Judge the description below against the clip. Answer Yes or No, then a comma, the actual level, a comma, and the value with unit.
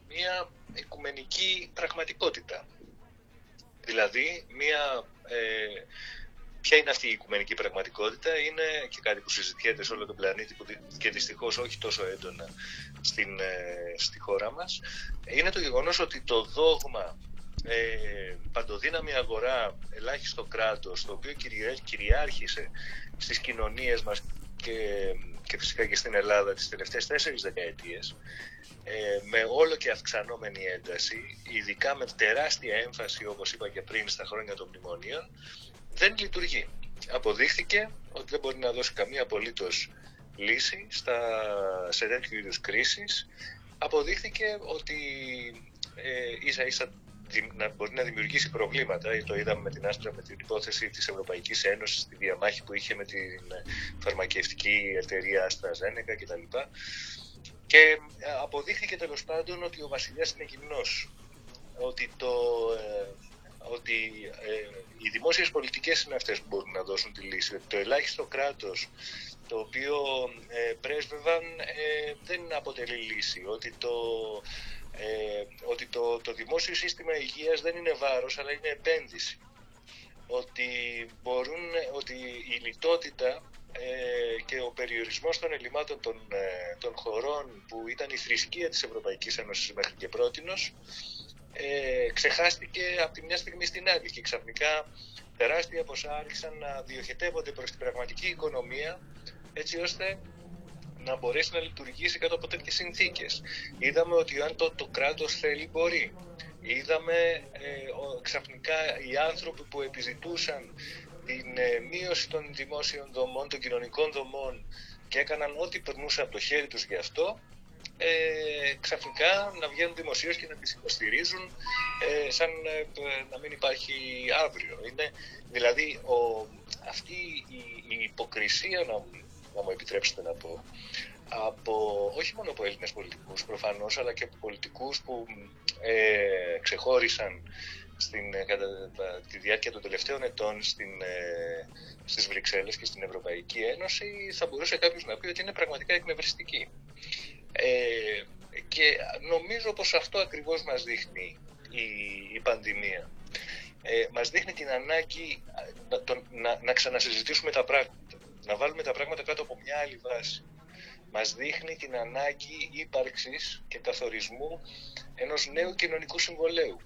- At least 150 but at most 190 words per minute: No, average, 135 wpm